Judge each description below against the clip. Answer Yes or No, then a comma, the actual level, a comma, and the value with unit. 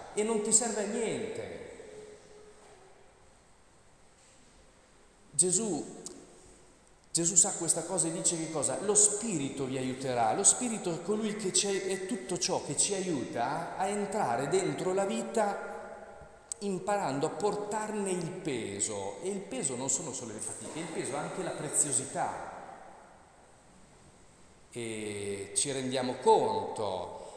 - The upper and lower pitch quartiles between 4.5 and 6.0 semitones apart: Yes, average, 4.9 semitones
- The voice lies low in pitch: No, high, 195 Hz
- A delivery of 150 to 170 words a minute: No, average, 130 wpm